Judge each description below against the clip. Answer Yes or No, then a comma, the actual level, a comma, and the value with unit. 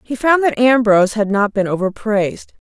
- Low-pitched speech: No, high, 220 Hz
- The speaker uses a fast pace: No, average, 180 wpm